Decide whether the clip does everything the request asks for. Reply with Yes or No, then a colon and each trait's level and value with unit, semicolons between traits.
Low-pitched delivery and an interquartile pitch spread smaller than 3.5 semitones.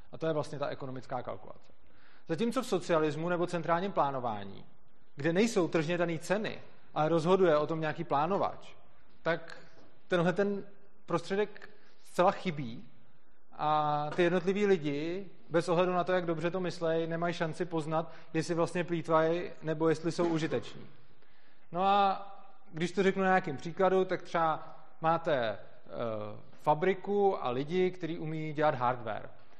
No: medium, 170 Hz; average, 2.8 semitones